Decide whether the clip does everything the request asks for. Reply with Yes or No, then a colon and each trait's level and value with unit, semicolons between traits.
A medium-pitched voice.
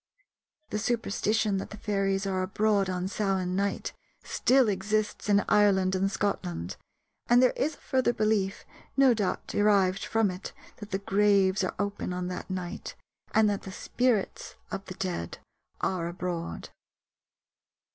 No: high, 195 Hz